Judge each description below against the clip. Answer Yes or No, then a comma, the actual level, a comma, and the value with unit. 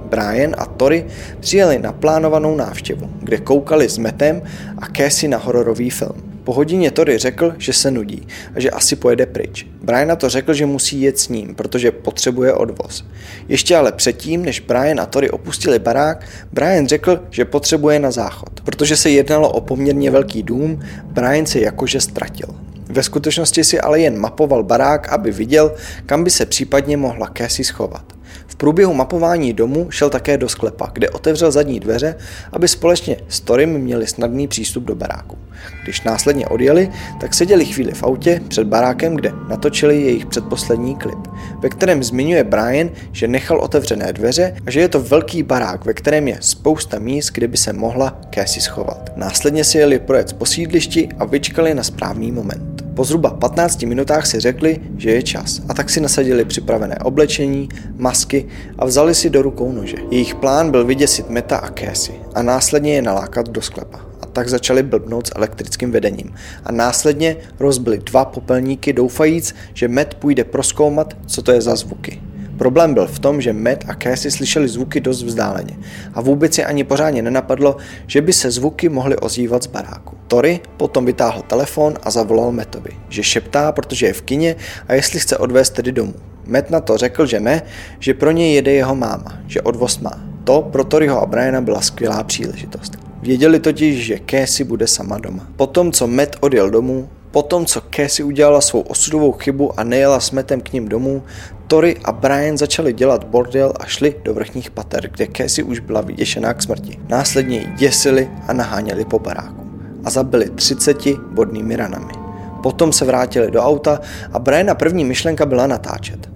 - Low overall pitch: Yes, low, 130 Hz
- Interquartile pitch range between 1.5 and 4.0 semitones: No, average, 4.6 semitones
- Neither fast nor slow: No, fast, 175 wpm